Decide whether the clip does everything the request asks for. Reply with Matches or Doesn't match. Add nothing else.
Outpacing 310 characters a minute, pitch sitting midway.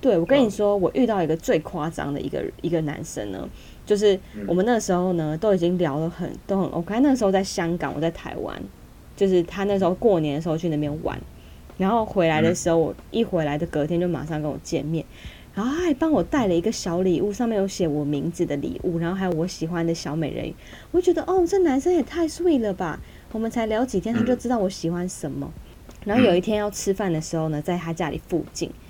Matches